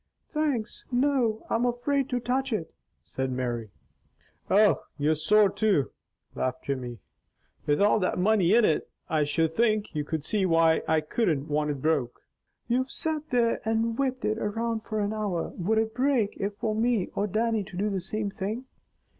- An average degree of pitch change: No, wide, 6.3 semitones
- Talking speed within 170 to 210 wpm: Yes, average, 180 wpm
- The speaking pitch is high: Yes, high, 210 Hz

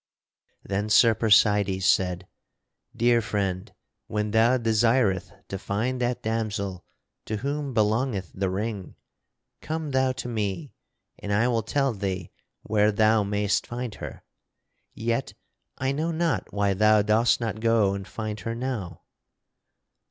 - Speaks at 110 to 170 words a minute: Yes, slow, 135 wpm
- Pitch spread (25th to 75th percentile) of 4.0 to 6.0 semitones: No, average, 3.0 semitones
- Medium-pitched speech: No, low, 110 Hz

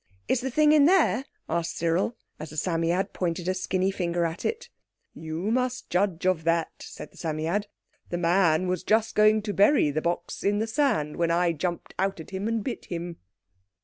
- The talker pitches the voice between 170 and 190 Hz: Yes, medium, 185 Hz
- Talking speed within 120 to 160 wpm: No, average, 195 wpm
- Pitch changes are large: No, average, 4.2 semitones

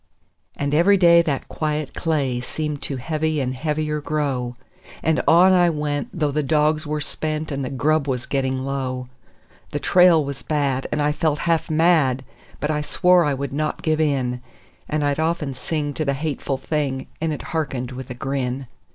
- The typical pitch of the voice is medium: Yes, medium, 150 Hz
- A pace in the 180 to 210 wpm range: Yes, average, 185 wpm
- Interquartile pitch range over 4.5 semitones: No, narrow, 2.5 semitones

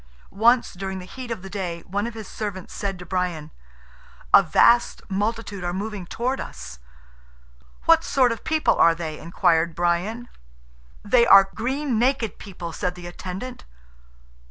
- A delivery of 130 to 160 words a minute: Yes, average, 155 wpm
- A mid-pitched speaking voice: No, high, 195 Hz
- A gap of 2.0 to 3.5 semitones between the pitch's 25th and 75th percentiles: No, average, 4.8 semitones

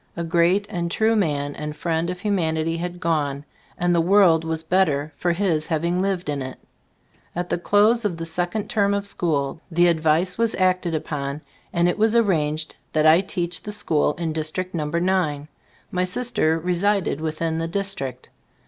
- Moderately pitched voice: Yes, medium, 170 Hz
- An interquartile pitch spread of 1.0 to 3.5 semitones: Yes, average, 3.0 semitones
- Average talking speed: Yes, average, 175 wpm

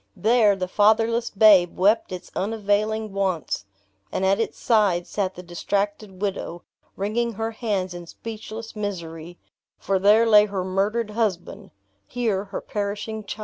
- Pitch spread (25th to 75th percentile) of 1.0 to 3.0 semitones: Yes, narrow, 2.6 semitones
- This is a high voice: Yes, high, 205 Hz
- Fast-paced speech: No, average, 145 wpm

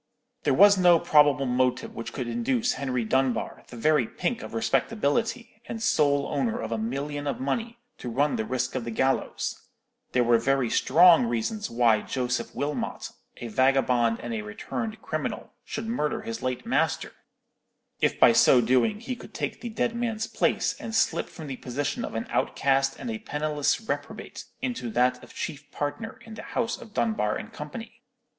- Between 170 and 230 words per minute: Yes, average, 180 wpm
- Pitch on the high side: No, medium, 140 Hz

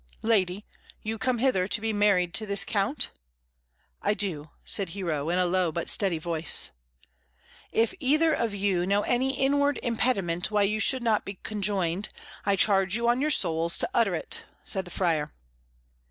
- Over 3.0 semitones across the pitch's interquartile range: Yes, average, 4.2 semitones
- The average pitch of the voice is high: Yes, high, 200 Hz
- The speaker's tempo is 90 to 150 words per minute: No, average, 170 wpm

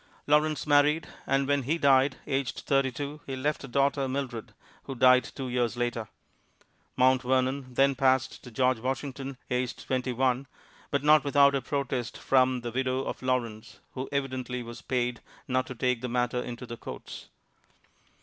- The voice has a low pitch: Yes, low, 130 Hz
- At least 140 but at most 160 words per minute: No, average, 170 wpm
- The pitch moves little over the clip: Yes, narrow, 1.8 semitones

